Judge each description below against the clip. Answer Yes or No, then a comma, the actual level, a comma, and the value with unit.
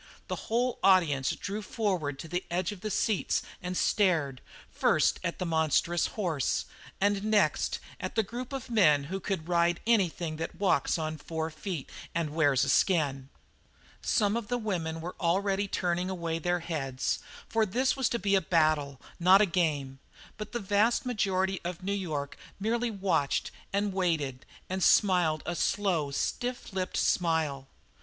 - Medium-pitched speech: Yes, medium, 180 Hz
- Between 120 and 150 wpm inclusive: No, average, 165 wpm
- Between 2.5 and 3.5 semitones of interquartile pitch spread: No, average, 4.4 semitones